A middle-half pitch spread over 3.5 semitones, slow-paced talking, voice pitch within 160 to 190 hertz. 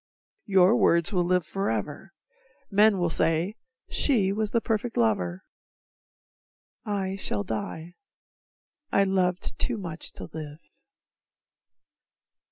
Yes: average, 4.1 semitones; slow, 105 wpm; medium, 185 Hz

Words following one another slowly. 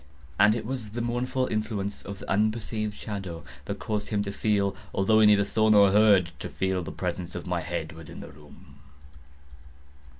No: average, 170 wpm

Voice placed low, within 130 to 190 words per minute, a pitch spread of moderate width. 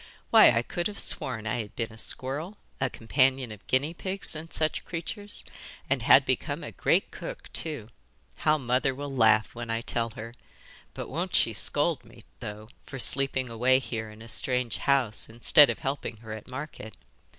Yes: low, 130 Hz; average, 185 wpm; average, 4.5 semitones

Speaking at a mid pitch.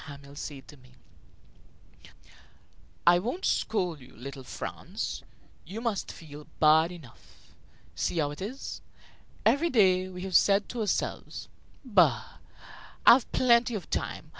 Yes: medium, 180 Hz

